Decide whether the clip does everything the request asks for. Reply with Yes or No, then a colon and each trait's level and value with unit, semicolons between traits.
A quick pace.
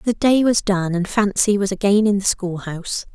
Yes: fast, 230 wpm